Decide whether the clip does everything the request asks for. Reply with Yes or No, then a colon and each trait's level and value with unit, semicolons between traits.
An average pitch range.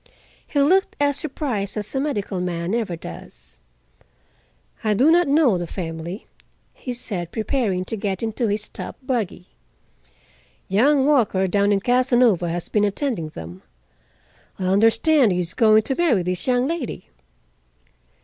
No: wide, 6.3 semitones